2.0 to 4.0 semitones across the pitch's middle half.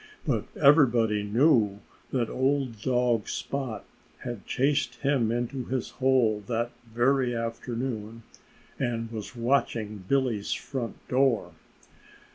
Yes: average, 2.7 semitones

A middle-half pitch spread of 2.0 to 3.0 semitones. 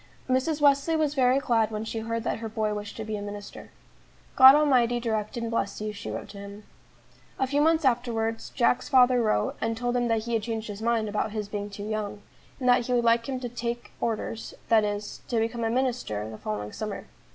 Yes: average, 2.7 semitones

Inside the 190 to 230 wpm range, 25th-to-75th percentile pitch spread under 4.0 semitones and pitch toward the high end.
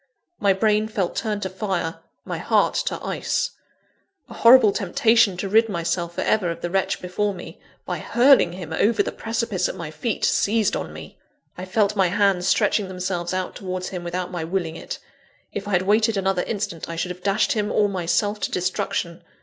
Yes: average, 195 wpm; average, 3.1 semitones; high, 195 Hz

